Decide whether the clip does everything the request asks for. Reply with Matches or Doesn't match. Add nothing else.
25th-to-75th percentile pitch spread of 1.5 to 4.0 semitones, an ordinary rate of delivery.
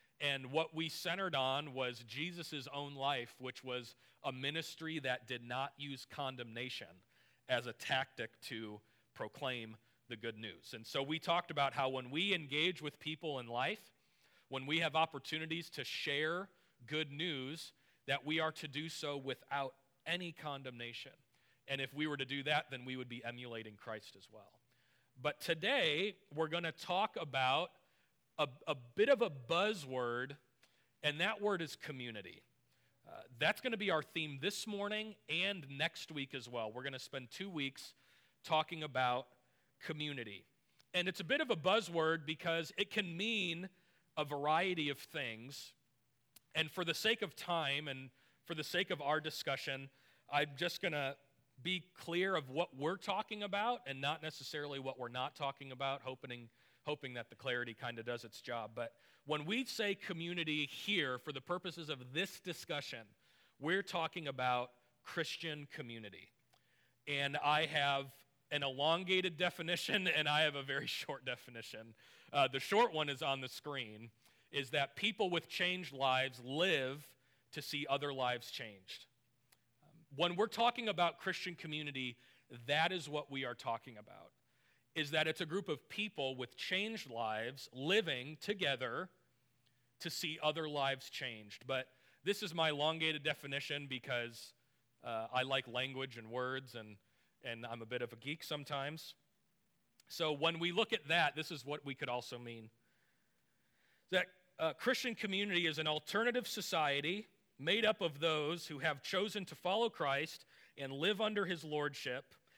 Doesn't match